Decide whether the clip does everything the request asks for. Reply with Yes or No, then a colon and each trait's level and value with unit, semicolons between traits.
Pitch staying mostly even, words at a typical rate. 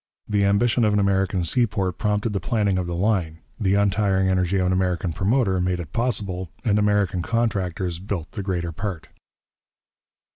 Yes: narrow, 2.3 semitones; average, 170 wpm